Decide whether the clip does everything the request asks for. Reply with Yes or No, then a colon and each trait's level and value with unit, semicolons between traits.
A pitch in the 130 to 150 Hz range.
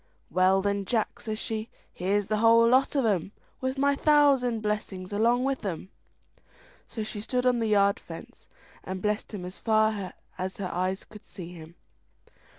No: high, 215 Hz